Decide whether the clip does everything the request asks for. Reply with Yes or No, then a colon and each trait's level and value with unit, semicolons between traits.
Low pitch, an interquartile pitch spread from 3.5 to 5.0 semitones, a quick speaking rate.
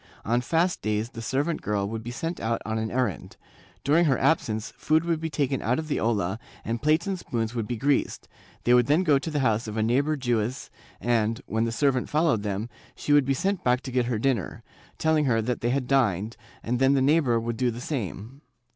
Yes: low, 125 Hz; average, 4.5 semitones; fast, 230 wpm